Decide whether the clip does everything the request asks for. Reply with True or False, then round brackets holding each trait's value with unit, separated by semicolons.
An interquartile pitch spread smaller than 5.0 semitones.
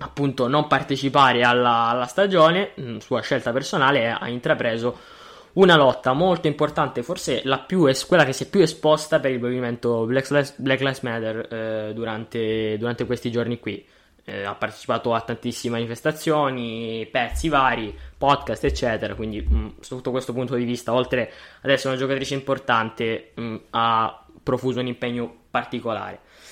True (3.0 semitones)